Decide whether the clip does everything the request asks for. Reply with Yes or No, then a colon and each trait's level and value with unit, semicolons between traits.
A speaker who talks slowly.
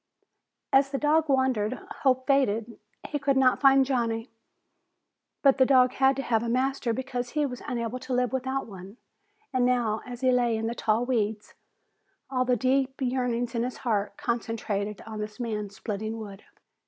No: average, 175 wpm